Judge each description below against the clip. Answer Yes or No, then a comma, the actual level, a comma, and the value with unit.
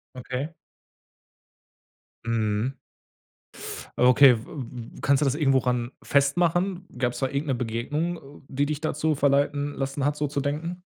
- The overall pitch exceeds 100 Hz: Yes, medium, 140 Hz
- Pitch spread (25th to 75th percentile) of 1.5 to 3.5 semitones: Yes, average, 2.8 semitones